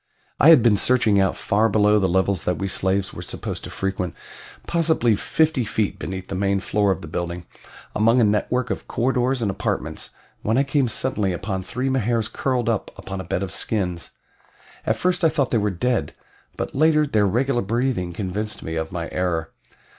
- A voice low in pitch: Yes, low, 105 Hz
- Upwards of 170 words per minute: Yes, average, 190 wpm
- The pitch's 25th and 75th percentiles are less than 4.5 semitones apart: No, average, 4.8 semitones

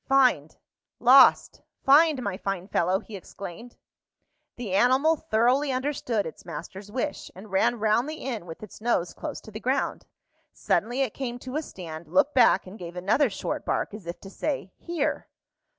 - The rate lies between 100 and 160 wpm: No, average, 170 wpm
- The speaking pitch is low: No, high, 230 Hz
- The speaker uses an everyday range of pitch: No, wide, 5.8 semitones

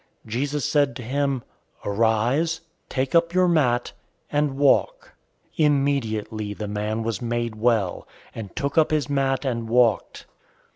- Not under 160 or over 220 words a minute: No, average, 145 wpm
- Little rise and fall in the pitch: No, average, 4.3 semitones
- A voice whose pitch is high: No, low, 130 Hz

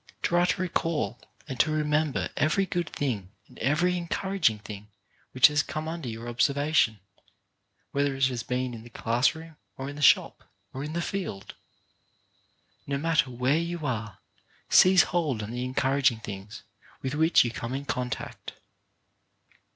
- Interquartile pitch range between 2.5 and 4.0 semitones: No, average, 5.0 semitones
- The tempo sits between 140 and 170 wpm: Yes, average, 160 wpm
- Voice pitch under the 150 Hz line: Yes, medium, 140 Hz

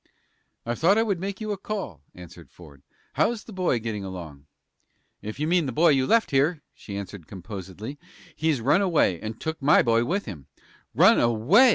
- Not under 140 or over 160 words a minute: No, average, 190 wpm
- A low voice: Yes, low, 130 Hz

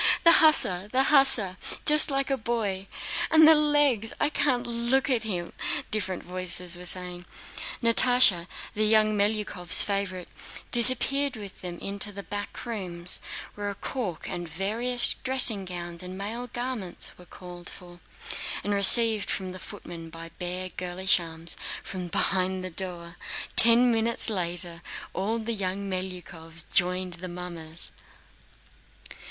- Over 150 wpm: No, average, 140 wpm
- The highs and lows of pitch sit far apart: No, average, 4.7 semitones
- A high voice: Yes, high, 195 Hz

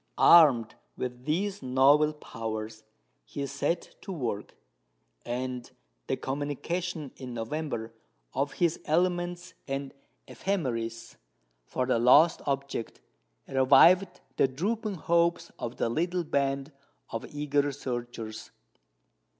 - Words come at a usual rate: No, slow, 105 wpm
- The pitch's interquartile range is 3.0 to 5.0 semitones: No, wide, 5.4 semitones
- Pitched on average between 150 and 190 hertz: No, medium, 140 Hz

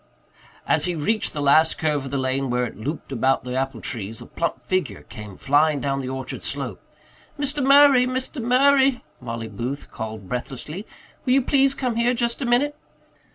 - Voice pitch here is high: No, medium, 150 Hz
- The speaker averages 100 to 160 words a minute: No, average, 185 wpm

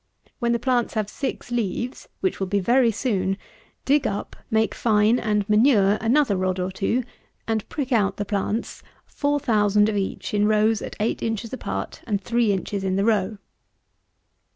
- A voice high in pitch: Yes, high, 215 Hz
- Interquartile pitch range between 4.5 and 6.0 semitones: No, average, 3.0 semitones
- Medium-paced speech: Yes, average, 170 wpm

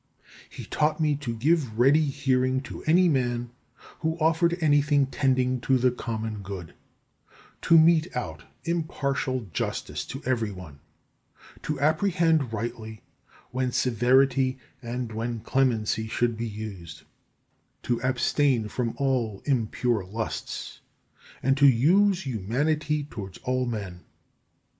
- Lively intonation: No, average, 4.5 semitones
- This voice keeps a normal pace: No, slow, 120 wpm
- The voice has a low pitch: Yes, low, 130 Hz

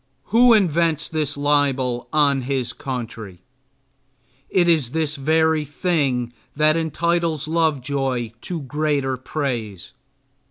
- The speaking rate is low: Yes, slow, 105 wpm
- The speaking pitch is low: No, medium, 145 Hz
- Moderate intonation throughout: Yes, average, 3.6 semitones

